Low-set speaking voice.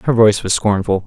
Yes: low, 105 Hz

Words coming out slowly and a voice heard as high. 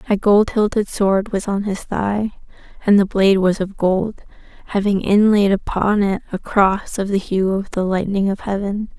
No: average, 185 wpm; high, 200 Hz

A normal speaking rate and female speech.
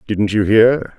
No: average, 185 wpm; male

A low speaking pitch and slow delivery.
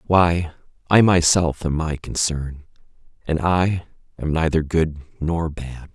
Yes: very low, 80 Hz; slow, 130 wpm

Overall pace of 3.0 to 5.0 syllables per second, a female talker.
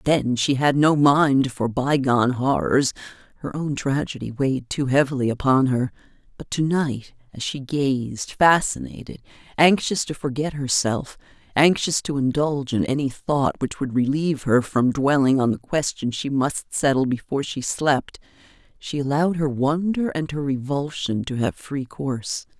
Yes: 4.6 syllables/s; female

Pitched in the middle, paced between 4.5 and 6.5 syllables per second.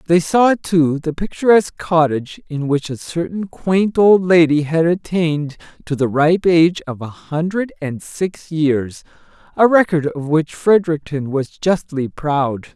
No: medium, 160 Hz; 4.3 syllables/s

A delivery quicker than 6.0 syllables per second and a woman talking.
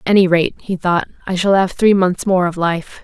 No: 5.2 syllables/s; female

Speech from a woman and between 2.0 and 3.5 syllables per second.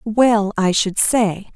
Yes: female; 2.8 syllables/s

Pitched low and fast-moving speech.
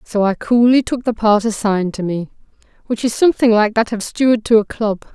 No: high, 220 Hz; fast, 220 wpm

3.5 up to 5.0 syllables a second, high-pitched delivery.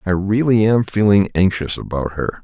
No: 4.9 syllables/s; low, 100 Hz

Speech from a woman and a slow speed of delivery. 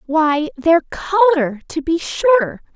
Yes: female; slow, 130 wpm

